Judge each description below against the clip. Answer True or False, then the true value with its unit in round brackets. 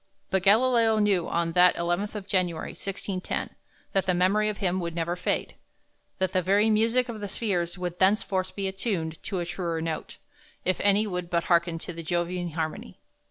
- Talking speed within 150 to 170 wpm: False (185 wpm)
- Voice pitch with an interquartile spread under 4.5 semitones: True (2.9 semitones)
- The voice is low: False (185 Hz)